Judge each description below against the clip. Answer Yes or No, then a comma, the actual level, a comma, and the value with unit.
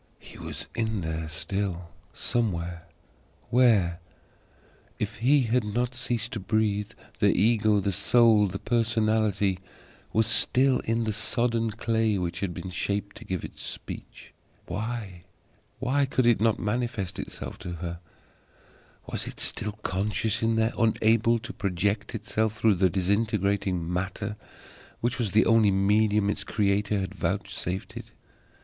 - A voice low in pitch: Yes, low, 105 Hz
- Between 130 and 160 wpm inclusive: Yes, slow, 135 wpm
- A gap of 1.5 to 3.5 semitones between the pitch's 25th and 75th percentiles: Yes, average, 2.8 semitones